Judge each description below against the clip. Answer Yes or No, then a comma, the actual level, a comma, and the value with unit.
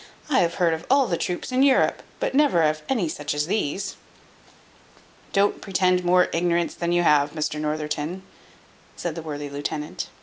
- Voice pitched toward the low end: No, medium, 170 Hz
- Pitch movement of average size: Yes, average, 3.6 semitones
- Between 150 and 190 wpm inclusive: Yes, average, 175 wpm